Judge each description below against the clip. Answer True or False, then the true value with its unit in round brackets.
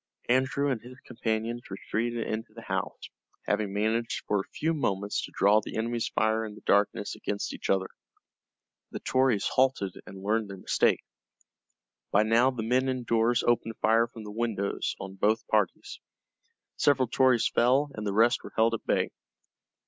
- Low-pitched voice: True (115 Hz)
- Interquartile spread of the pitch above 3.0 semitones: False (2.7 semitones)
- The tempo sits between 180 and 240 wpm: False (165 wpm)